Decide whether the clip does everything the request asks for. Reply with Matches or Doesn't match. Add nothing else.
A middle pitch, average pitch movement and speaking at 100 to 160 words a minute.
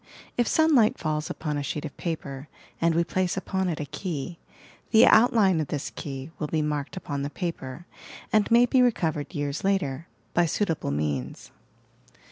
Doesn't match